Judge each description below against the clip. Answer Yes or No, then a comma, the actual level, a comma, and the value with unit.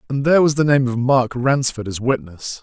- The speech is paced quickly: Yes, fast, 230 wpm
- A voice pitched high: No, low, 125 Hz